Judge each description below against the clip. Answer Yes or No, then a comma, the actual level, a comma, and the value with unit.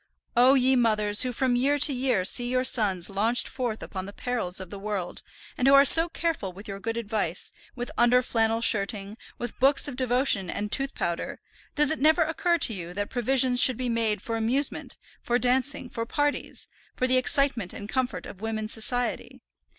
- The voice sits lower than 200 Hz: No, high, 240 Hz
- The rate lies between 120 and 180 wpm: No, average, 195 wpm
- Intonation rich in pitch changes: No, average, 3.8 semitones